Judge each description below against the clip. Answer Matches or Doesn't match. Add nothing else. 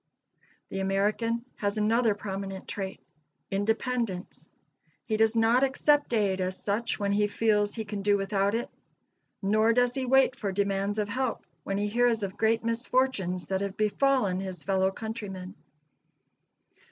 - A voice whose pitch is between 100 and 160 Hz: Doesn't match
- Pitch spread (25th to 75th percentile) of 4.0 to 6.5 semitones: Doesn't match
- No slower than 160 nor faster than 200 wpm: Doesn't match